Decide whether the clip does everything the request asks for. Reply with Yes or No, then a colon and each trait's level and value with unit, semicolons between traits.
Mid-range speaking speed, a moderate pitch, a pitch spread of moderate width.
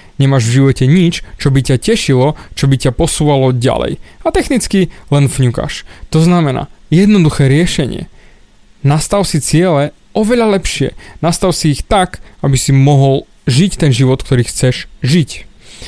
Yes: average, 145 wpm; medium, 145 Hz; average, 4.4 semitones